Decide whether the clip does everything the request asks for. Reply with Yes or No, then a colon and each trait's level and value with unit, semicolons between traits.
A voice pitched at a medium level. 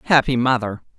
No: low, 125 Hz